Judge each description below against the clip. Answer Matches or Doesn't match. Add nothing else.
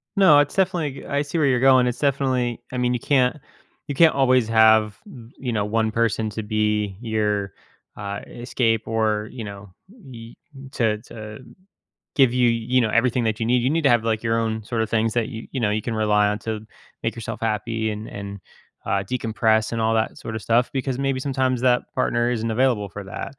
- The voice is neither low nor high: Doesn't match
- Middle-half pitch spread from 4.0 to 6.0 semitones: Doesn't match